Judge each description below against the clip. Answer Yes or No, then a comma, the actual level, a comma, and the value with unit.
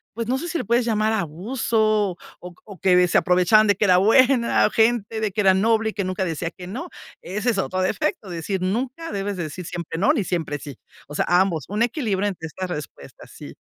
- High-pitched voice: Yes, high, 195 Hz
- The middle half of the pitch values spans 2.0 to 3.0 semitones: No, average, 3.7 semitones